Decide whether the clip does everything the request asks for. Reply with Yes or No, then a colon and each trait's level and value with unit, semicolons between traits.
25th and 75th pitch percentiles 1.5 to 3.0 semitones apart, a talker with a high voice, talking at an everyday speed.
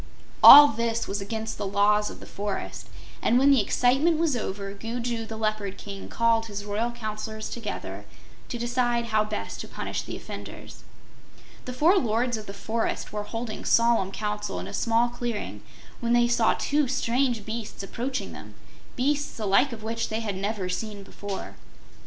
Yes: narrow, 2.5 semitones; high, 225 Hz; average, 175 wpm